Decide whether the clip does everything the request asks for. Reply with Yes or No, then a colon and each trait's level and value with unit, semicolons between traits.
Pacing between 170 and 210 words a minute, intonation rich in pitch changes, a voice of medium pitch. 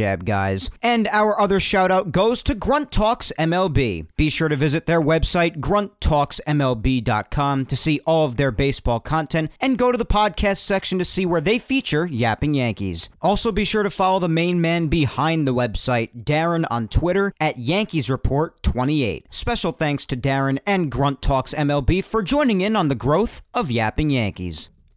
Yes: average, 175 wpm; wide, 6.7 semitones; medium, 155 Hz